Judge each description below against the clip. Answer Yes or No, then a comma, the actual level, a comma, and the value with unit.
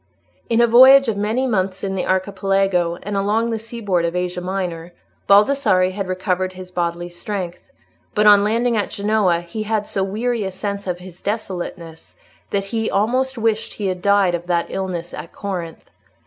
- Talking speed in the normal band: Yes, average, 175 wpm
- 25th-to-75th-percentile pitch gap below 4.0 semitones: Yes, average, 3.2 semitones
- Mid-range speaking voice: No, high, 195 Hz